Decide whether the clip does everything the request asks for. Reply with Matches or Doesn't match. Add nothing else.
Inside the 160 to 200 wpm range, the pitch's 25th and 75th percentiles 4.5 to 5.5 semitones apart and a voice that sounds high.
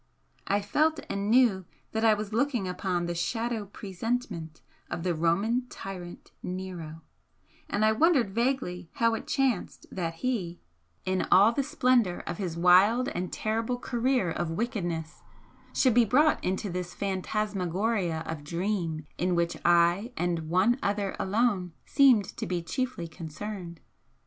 Doesn't match